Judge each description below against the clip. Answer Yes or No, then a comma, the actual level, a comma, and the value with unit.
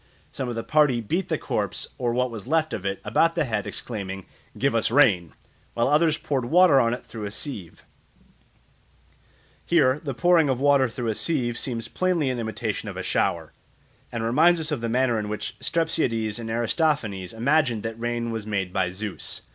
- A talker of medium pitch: No, low, 120 Hz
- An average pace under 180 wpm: No, average, 190 wpm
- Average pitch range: Yes, average, 5.0 semitones